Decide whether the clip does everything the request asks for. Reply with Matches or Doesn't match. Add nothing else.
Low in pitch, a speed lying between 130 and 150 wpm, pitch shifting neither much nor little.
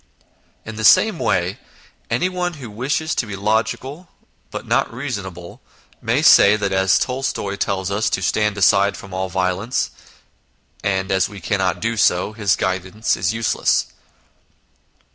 Matches